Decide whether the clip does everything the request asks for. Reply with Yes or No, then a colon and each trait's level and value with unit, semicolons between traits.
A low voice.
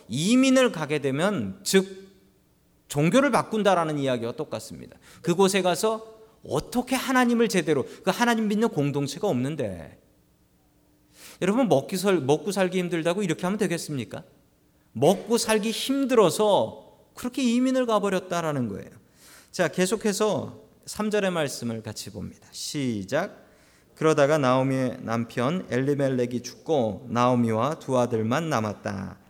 No: medium, 165 Hz